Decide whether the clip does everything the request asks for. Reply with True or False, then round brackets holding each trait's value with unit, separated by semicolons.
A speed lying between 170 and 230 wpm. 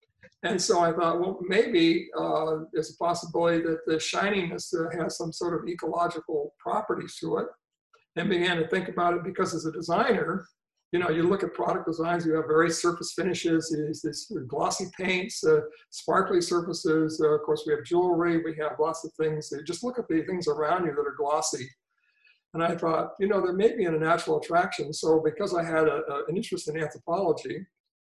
True (205 wpm)